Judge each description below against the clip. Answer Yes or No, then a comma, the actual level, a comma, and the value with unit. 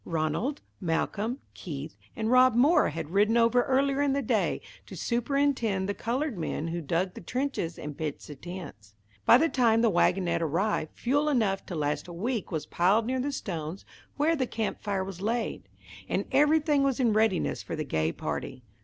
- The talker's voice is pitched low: No, high, 215 Hz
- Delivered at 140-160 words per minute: No, average, 185 wpm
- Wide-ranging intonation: Yes, wide, 7.3 semitones